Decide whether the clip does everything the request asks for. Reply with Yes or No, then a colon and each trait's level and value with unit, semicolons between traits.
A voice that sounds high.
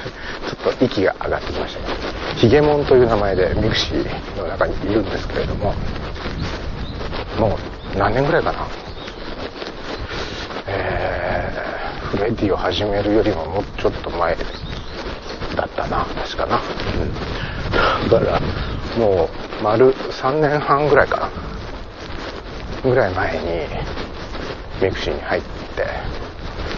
No: very low, 95 Hz